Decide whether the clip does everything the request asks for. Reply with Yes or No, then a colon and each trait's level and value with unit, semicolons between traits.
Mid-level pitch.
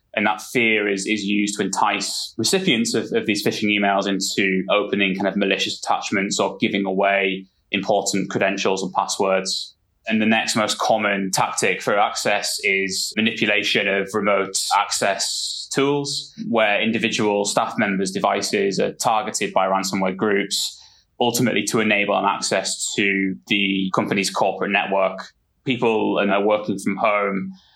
No: low, 100 Hz